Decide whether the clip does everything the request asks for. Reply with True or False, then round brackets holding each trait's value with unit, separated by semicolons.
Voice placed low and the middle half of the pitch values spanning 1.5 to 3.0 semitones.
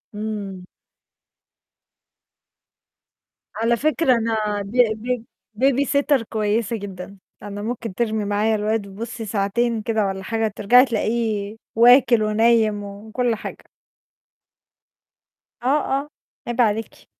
False (220 Hz; 2.4 semitones)